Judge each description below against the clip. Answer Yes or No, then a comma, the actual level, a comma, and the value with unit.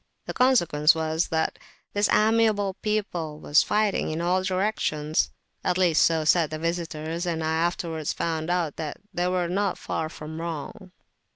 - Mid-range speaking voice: Yes, medium, 170 Hz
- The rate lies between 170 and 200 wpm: No, average, 155 wpm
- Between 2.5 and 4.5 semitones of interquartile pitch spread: Yes, average, 2.9 semitones